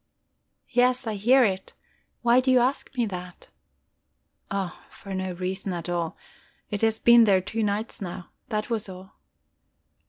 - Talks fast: No, average, 155 wpm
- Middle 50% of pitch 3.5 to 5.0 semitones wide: Yes, average, 4.1 semitones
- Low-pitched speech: No, high, 205 Hz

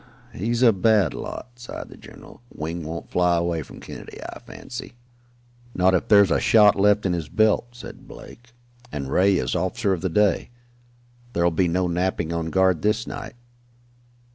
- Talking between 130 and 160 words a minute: No, average, 170 wpm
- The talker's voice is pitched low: Yes, very low, 95 Hz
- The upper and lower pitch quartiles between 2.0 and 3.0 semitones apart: No, average, 3.9 semitones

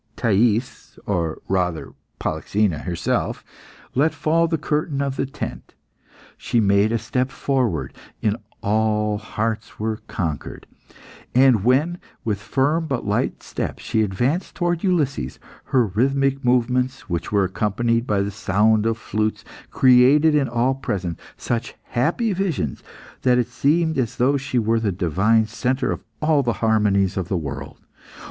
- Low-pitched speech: Yes, low, 115 Hz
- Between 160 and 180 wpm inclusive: No, average, 145 wpm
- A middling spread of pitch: Yes, average, 4.8 semitones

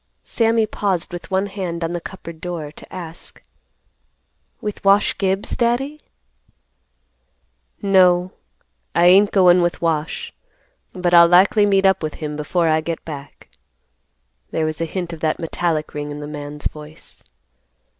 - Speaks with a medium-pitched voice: Yes, medium, 175 Hz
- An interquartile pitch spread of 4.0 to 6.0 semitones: No, average, 3.5 semitones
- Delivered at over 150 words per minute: No, average, 145 wpm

